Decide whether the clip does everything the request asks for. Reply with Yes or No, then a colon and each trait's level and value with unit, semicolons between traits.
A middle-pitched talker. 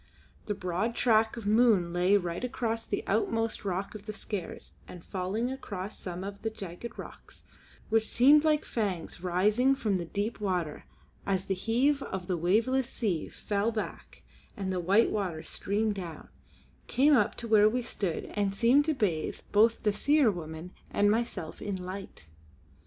No: high, 205 Hz